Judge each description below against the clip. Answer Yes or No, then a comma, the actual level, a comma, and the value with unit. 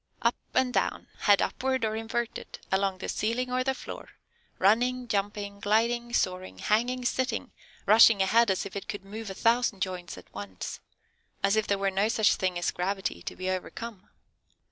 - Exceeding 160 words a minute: Yes, average, 175 wpm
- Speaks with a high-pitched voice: Yes, high, 210 Hz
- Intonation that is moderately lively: Yes, average, 3.5 semitones